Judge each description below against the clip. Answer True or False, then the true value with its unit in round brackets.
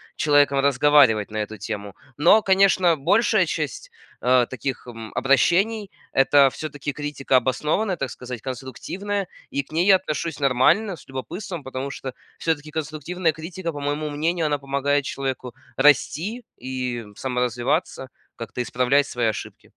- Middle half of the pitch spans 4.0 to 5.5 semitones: True (4.4 semitones)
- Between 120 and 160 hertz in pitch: True (140 Hz)